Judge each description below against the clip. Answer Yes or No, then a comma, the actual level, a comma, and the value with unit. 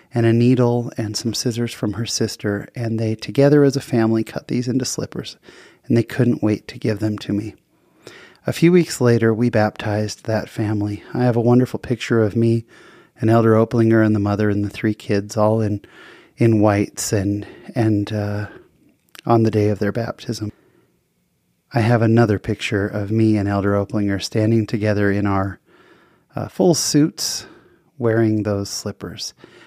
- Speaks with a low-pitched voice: Yes, low, 110 Hz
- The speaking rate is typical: Yes, average, 170 wpm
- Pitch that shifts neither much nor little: No, narrow, 2.2 semitones